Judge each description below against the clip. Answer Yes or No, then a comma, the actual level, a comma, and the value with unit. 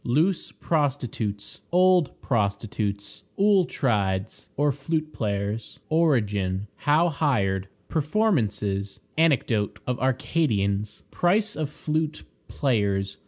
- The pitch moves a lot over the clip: Yes, wide, 7.7 semitones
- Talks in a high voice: No, low, 125 Hz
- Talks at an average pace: No, slow, 85 wpm